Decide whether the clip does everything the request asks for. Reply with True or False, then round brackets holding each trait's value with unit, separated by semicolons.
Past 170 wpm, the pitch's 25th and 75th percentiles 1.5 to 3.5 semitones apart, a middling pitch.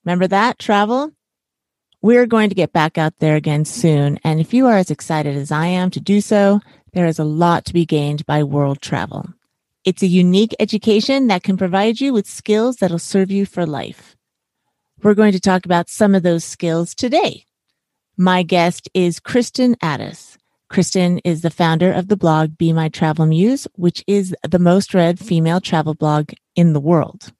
False (190 wpm; 4.1 semitones; 180 Hz)